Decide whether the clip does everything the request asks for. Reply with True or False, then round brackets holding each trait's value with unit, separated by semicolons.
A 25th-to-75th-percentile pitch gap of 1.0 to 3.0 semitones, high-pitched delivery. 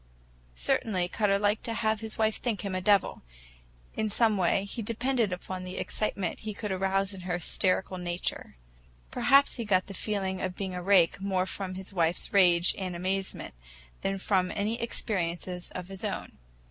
True (2.5 semitones; 195 Hz)